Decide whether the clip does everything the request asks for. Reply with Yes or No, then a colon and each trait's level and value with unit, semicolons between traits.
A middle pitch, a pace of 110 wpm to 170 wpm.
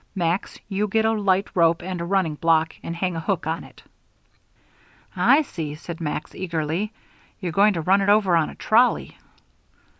No: medium, 180 Hz; average, 180 wpm